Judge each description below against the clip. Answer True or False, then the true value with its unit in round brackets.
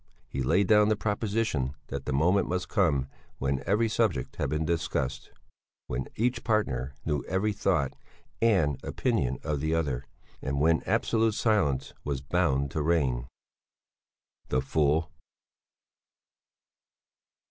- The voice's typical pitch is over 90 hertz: False (80 Hz)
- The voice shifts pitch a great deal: True (6.8 semitones)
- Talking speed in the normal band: False (125 wpm)